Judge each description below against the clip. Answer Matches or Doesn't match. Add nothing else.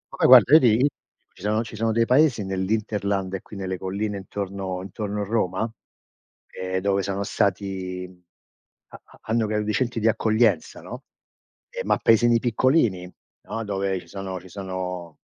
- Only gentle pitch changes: Doesn't match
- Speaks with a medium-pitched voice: Doesn't match